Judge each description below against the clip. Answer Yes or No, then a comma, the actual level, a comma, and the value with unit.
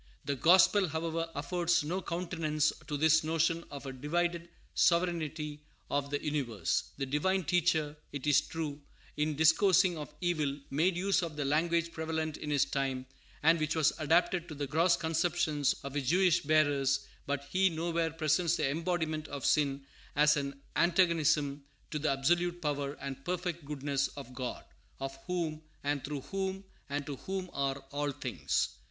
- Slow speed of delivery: No, average, 160 wpm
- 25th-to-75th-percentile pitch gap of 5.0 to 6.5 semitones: No, average, 3.1 semitones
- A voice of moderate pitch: Yes, medium, 155 Hz